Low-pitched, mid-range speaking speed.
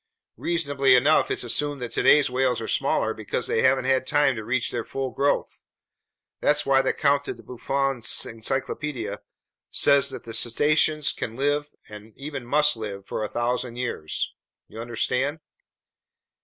Yes: low, 130 Hz; average, 150 wpm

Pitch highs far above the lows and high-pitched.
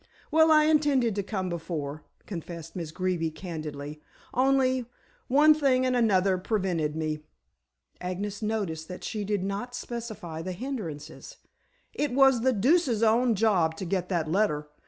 Yes: wide, 6.8 semitones; high, 200 Hz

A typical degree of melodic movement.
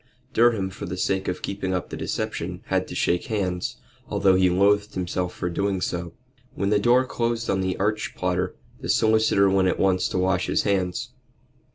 No: narrow, 2.0 semitones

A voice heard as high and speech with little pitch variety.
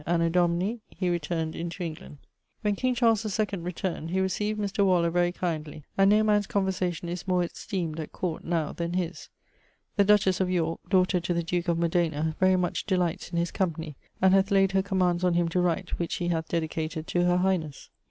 No: medium, 175 Hz; narrow, 2.2 semitones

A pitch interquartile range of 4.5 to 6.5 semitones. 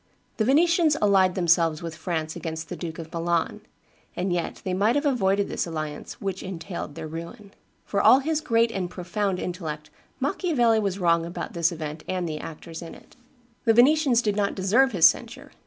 Yes: average, 5.2 semitones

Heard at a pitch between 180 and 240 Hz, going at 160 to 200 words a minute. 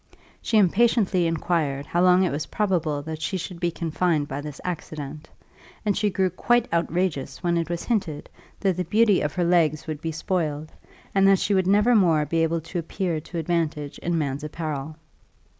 No: medium, 170 Hz; average, 190 wpm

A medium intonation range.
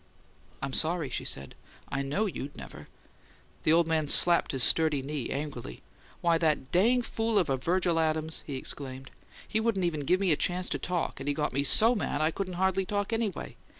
Yes: average, 4.7 semitones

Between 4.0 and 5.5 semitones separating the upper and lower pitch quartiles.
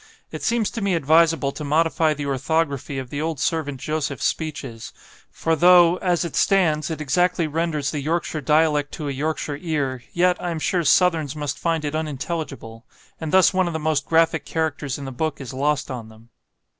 No: average, 2.7 semitones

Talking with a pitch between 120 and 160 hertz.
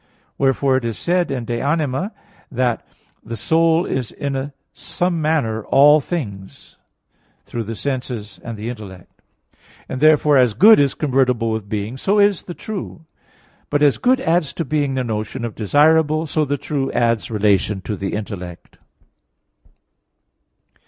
Yes: low, 135 Hz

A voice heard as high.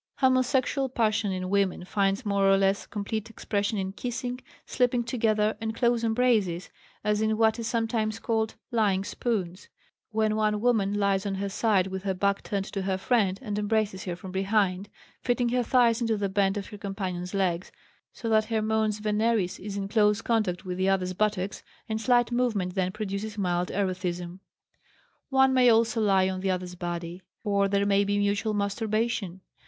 Yes: high, 205 Hz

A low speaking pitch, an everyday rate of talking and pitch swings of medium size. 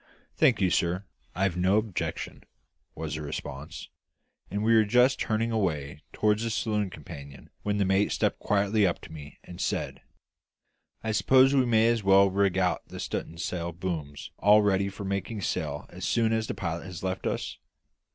Yes: low, 100 Hz; average, 175 wpm; average, 3.9 semitones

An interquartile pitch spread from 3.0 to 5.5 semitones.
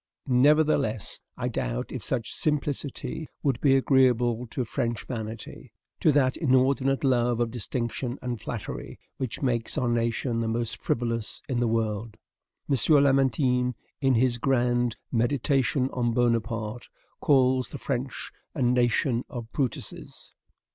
No: narrow, 2.4 semitones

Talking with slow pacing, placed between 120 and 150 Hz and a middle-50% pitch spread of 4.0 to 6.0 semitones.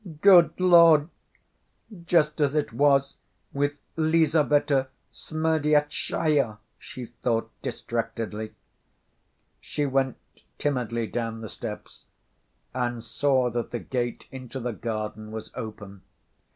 Yes: slow, 100 wpm; low, 130 Hz; average, 4.5 semitones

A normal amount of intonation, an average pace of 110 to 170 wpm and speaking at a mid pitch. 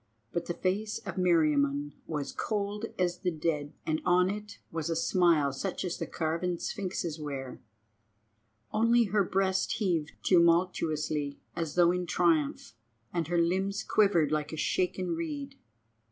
Yes: average, 3.6 semitones; average, 145 wpm; medium, 175 Hz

